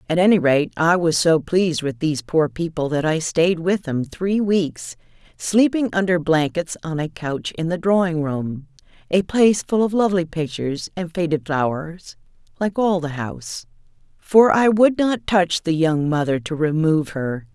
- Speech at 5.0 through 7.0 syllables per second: No, 4.6 syllables/s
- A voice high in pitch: No, medium, 170 Hz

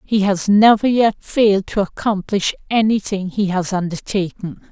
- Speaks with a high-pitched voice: Yes, high, 200 Hz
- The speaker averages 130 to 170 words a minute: Yes, average, 140 wpm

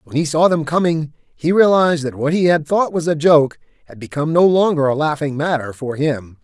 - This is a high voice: No, medium, 155 Hz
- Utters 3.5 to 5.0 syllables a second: No, 5.4 syllables/s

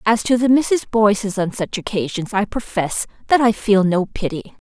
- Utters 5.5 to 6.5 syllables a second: No, 4.8 syllables/s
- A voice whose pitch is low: No, high, 210 Hz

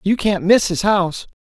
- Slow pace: No, fast, 205 wpm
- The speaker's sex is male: Yes, male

